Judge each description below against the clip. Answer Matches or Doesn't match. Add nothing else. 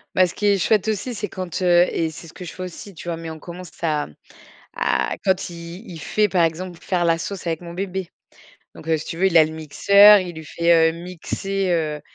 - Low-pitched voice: Doesn't match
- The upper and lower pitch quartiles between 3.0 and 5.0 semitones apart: Doesn't match